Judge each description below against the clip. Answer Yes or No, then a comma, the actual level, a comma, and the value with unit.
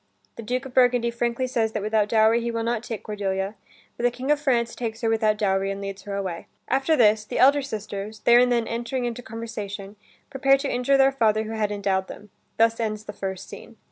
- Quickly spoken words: Yes, fast, 225 wpm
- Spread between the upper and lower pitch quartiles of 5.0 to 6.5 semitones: No, average, 2.7 semitones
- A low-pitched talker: No, high, 225 Hz